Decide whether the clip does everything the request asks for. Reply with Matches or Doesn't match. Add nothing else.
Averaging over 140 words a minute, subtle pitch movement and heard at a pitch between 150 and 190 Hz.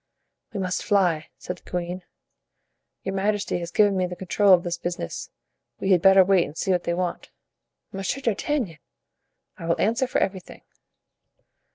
Matches